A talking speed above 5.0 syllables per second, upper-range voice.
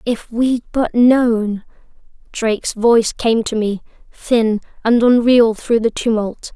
No: 3.7 syllables/s; high, 230 Hz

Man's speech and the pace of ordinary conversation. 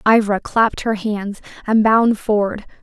No: female; average, 150 wpm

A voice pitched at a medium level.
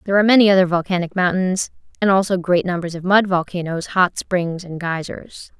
Yes: medium, 180 Hz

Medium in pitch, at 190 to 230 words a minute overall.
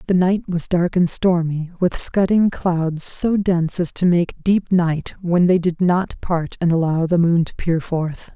Yes: medium, 175 Hz; average, 200 wpm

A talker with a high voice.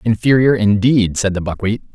No: low, 105 Hz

